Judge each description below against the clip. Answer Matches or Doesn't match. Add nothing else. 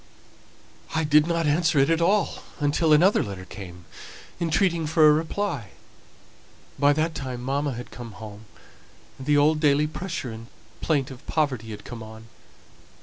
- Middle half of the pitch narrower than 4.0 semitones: Doesn't match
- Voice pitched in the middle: Matches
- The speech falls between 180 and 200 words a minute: Doesn't match